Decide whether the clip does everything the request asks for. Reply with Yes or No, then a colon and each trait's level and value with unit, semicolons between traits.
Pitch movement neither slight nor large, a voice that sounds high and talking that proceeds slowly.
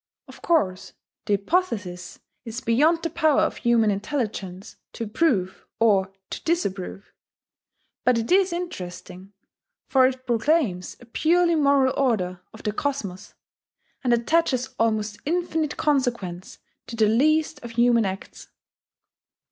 No: wide, 7.0 semitones; high, 235 Hz; slow, 125 wpm